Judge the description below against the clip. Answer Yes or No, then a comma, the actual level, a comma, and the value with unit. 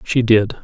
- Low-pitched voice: Yes, low, 110 Hz